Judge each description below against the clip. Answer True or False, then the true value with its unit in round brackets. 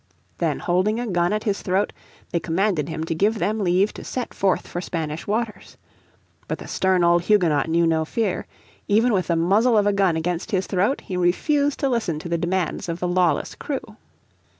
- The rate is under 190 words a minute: False (200 wpm)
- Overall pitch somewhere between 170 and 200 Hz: True (185 Hz)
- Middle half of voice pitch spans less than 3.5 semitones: False (3.8 semitones)